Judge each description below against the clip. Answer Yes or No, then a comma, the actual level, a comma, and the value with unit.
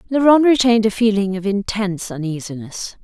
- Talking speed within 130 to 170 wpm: Yes, average, 140 wpm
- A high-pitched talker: Yes, high, 210 Hz